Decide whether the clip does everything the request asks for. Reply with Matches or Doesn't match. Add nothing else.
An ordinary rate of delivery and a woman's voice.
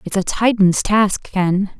Matches